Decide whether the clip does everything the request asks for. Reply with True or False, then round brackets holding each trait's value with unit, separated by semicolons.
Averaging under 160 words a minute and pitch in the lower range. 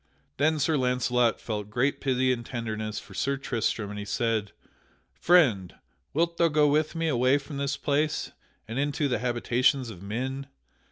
False (165 wpm; 130 Hz)